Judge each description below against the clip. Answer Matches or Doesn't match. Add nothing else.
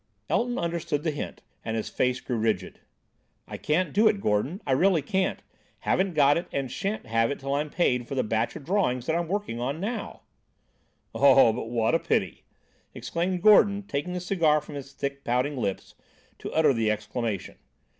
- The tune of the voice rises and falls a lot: Matches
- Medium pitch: Matches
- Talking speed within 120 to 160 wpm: Doesn't match